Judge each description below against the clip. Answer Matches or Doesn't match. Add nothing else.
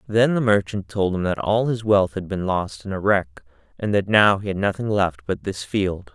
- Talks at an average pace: Doesn't match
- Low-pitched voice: Matches